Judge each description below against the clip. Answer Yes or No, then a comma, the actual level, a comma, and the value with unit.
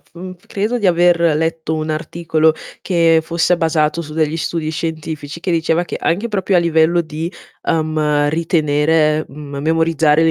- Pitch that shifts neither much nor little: No, narrow, 1.6 semitones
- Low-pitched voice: No, medium, 160 Hz